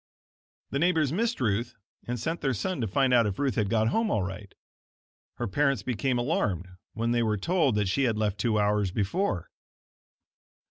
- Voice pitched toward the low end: Yes, low, 120 Hz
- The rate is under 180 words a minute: No, average, 185 wpm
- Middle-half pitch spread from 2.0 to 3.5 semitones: No, average, 5.0 semitones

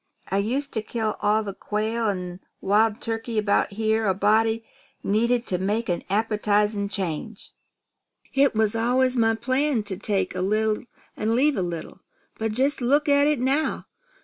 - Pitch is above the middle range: Yes, high, 220 Hz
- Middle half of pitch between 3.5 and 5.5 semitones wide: No, average, 2.8 semitones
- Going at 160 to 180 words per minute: Yes, average, 165 wpm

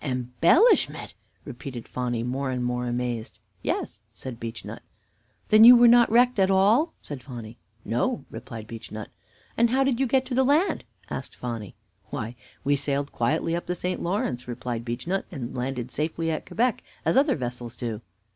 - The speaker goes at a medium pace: Yes, average, 165 wpm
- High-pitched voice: No, low, 135 Hz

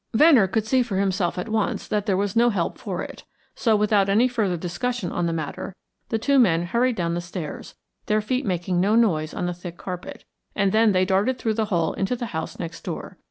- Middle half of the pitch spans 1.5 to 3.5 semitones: No, average, 4.3 semitones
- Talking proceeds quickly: Yes, fast, 225 wpm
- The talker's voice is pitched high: Yes, high, 195 Hz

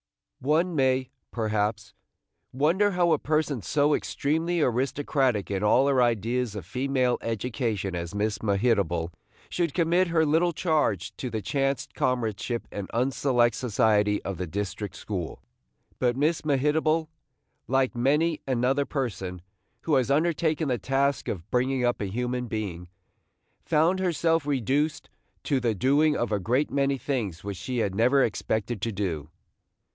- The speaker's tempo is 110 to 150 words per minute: Yes, average, 145 wpm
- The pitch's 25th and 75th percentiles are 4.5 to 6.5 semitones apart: Yes, wide, 5.6 semitones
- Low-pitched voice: Yes, low, 125 Hz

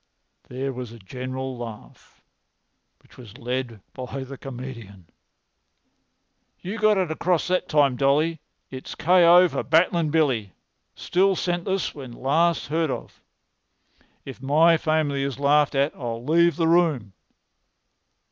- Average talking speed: No, slow, 125 wpm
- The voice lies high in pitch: No, medium, 140 Hz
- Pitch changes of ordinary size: Yes, average, 4.7 semitones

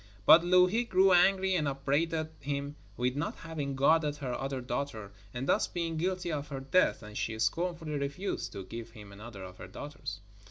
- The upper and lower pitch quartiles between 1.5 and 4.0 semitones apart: No, average, 5.3 semitones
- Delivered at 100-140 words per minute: No, average, 185 wpm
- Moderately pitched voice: Yes, medium, 145 Hz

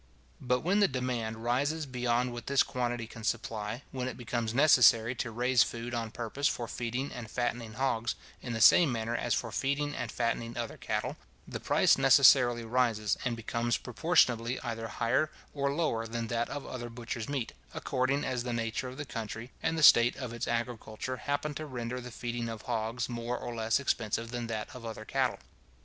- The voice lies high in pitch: No, low, 120 Hz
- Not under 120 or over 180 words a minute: No, average, 190 wpm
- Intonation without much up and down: Yes, narrow, 2.0 semitones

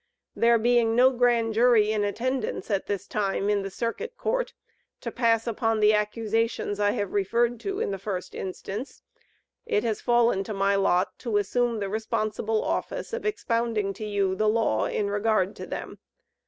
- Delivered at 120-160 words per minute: No, average, 175 wpm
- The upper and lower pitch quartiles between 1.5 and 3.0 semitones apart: Yes, narrow, 2.6 semitones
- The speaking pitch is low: No, high, 220 Hz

